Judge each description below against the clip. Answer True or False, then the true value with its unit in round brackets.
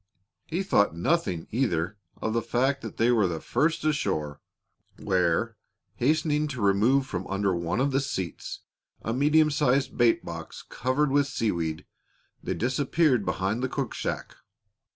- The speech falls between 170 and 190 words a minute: False (145 wpm)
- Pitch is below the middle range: True (125 Hz)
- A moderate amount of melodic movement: False (6.8 semitones)